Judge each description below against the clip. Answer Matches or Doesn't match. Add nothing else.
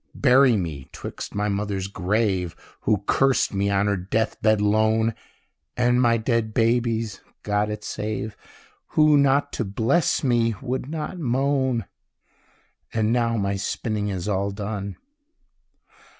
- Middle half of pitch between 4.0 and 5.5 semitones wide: Doesn't match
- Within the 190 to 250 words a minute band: Doesn't match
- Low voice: Matches